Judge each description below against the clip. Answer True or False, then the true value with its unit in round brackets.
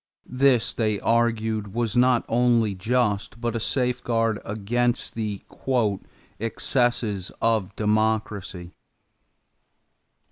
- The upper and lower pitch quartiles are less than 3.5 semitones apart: True (2.4 semitones)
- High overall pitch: False (115 Hz)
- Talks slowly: True (85 wpm)